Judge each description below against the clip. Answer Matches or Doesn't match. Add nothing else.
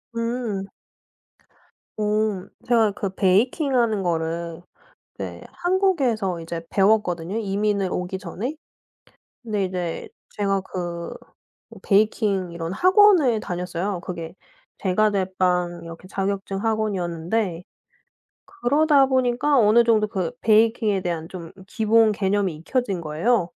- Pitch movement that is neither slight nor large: Matches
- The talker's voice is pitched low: Doesn't match